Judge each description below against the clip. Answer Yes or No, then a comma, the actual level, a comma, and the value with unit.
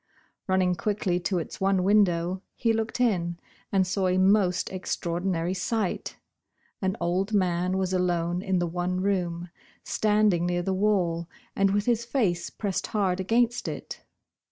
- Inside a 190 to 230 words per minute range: No, average, 150 wpm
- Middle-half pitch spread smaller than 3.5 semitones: Yes, narrow, 2.5 semitones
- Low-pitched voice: No, medium, 185 Hz